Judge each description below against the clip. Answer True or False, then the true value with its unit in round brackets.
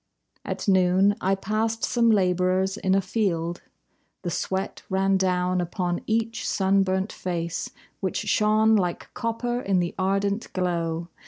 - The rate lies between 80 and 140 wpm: True (135 wpm)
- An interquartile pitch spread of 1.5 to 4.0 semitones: True (2.8 semitones)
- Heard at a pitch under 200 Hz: True (190 Hz)